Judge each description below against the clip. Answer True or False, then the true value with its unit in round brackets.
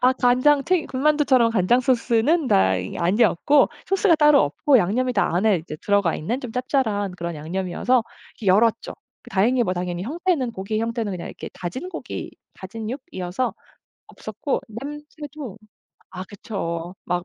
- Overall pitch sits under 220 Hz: False (230 Hz)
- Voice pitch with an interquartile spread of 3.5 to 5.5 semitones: False (6.3 semitones)